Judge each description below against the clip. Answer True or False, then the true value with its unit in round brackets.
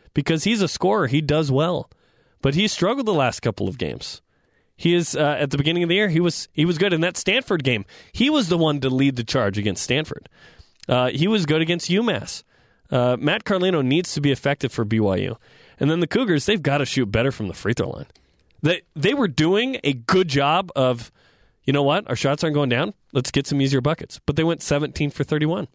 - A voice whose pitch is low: False (150 Hz)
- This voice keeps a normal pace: False (230 wpm)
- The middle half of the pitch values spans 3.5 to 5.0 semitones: True (4.5 semitones)